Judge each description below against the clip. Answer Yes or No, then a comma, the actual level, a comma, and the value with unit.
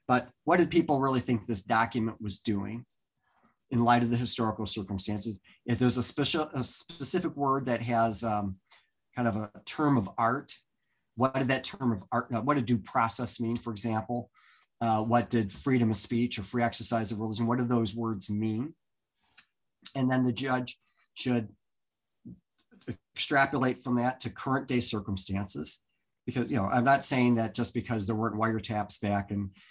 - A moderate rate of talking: Yes, average, 175 wpm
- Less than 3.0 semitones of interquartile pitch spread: Yes, narrow, 2.4 semitones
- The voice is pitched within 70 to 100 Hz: No, low, 120 Hz